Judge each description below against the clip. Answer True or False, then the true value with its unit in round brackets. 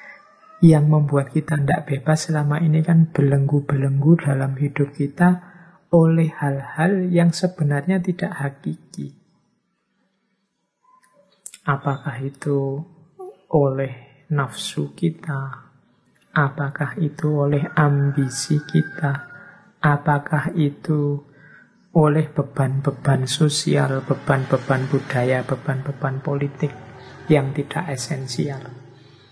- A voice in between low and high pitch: True (145 Hz)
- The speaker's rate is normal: False (80 wpm)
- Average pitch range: True (3.0 semitones)